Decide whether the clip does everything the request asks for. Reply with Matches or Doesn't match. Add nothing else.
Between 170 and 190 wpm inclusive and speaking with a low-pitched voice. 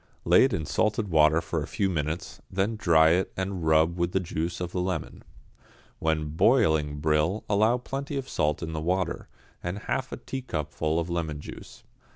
Matches